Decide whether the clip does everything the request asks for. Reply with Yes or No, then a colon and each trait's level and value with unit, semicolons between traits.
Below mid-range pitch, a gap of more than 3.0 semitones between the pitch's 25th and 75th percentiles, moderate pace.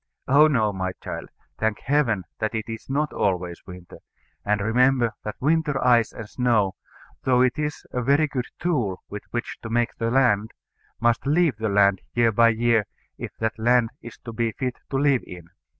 Yes: low, 115 Hz; average, 3.5 semitones; average, 185 wpm